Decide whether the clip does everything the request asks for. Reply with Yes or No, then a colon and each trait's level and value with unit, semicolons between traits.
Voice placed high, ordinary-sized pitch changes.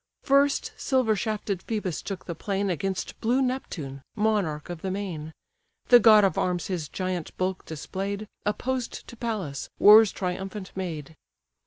Yes: high, 195 Hz; average, 3.6 semitones